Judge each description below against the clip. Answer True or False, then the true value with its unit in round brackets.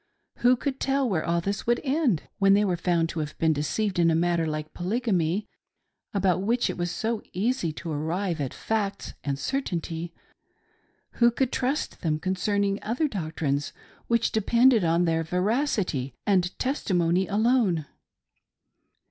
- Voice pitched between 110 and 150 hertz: False (190 Hz)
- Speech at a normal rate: True (150 wpm)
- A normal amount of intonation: False (5.8 semitones)